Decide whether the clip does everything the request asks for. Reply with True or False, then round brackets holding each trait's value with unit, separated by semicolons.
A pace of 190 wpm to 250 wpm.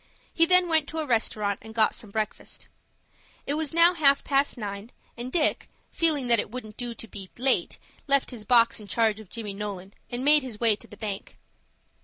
True (205 wpm)